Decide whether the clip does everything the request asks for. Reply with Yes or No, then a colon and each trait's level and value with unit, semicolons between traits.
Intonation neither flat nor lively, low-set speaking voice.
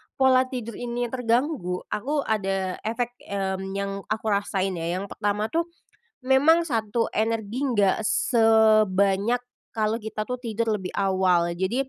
No: average, 3.8 semitones; high, 220 Hz